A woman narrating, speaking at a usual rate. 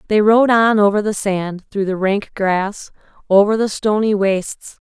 Yes: female; average, 170 wpm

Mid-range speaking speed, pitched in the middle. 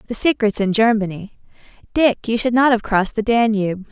No: average, 185 wpm; high, 220 Hz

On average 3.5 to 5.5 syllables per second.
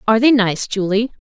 No: 6.0 syllables/s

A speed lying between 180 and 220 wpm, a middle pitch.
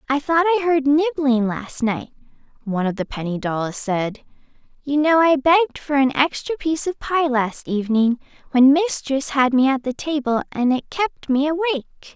No: average, 185 wpm; very high, 275 Hz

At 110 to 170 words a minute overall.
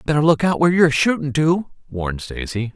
No: average, 195 wpm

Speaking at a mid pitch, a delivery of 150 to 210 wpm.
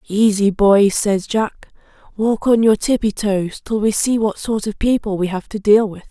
No: high, 210 Hz; fast, 205 wpm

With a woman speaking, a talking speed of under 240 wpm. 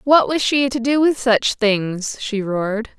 Yes: female; average, 200 wpm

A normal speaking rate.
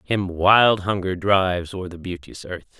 Yes: average, 170 wpm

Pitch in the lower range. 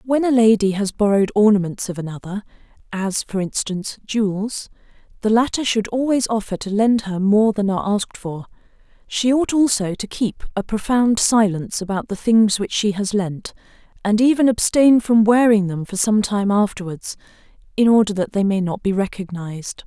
No: high, 210 Hz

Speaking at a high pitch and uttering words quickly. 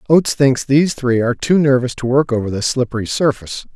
No: low, 130 Hz; fast, 210 wpm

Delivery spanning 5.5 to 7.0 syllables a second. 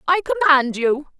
Yes: 5.6 syllables/s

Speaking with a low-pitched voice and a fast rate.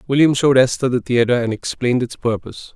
No: low, 125 Hz; average, 195 wpm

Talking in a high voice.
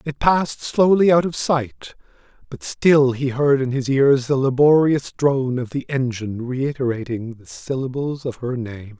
No: low, 135 Hz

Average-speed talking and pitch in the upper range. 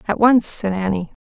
Yes: average, 195 wpm; high, 205 Hz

